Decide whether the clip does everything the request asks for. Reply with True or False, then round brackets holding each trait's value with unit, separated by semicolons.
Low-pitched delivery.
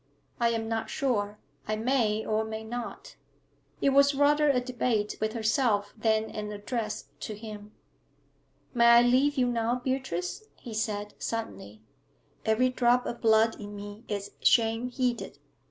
False (225 Hz)